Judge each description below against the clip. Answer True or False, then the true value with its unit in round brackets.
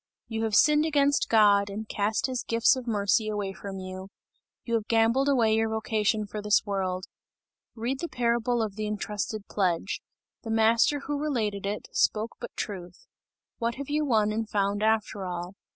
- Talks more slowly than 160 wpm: False (175 wpm)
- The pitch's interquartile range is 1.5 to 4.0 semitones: True (2.5 semitones)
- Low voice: False (220 Hz)